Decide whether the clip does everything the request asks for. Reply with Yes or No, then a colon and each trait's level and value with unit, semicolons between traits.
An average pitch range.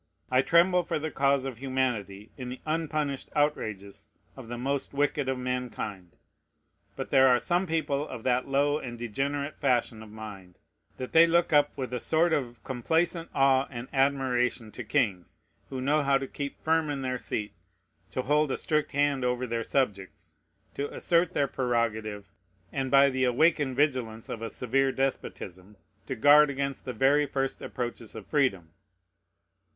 Yes: average, 3.3 semitones